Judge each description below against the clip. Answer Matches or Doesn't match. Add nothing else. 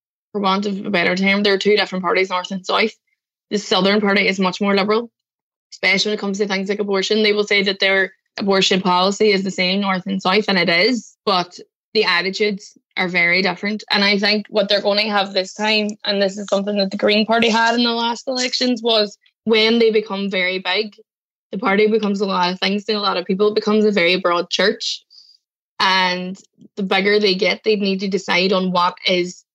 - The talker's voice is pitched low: Doesn't match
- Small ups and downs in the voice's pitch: Matches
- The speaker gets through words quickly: Matches